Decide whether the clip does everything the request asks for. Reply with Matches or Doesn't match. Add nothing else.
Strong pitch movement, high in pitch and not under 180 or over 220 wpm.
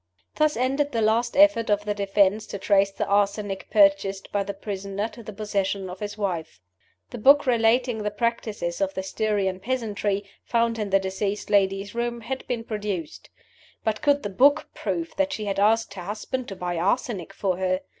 Doesn't match